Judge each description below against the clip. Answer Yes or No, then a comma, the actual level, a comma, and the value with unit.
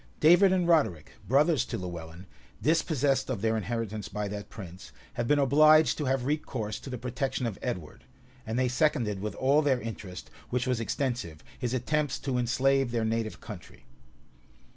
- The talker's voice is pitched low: Yes, low, 125 Hz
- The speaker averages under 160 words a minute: No, average, 165 wpm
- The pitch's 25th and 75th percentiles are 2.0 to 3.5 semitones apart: No, average, 4.7 semitones